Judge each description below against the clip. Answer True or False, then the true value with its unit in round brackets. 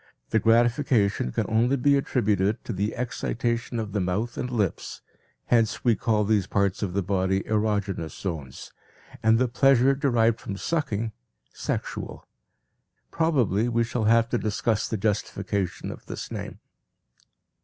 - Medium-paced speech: True (145 wpm)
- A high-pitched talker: False (110 Hz)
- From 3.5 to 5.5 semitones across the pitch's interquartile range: False (3.0 semitones)